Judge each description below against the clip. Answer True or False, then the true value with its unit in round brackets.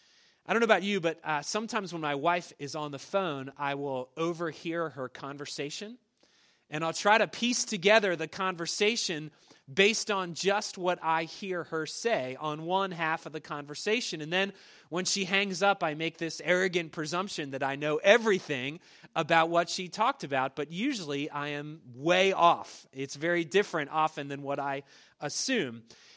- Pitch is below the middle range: False (165 Hz)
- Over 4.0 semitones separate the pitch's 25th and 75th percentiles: True (4.6 semitones)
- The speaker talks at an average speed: True (175 wpm)